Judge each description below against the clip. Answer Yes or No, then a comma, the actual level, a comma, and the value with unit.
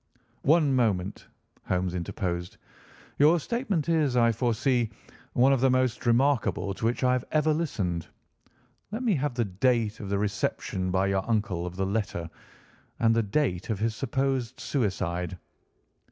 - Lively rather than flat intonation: Yes, wide, 5.7 semitones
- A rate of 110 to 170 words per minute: Yes, average, 155 wpm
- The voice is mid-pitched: No, low, 115 Hz